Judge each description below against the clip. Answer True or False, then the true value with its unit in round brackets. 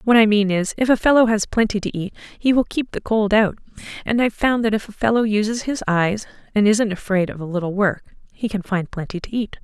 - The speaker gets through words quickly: True (250 wpm)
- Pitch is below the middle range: False (210 Hz)